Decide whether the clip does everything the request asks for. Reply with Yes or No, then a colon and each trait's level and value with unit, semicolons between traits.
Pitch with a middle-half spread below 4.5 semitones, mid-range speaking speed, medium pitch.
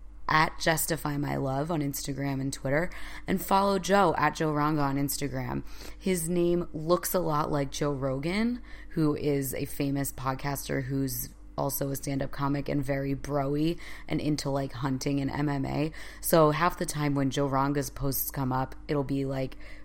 Yes: narrow, 2.4 semitones; average, 175 wpm; medium, 145 Hz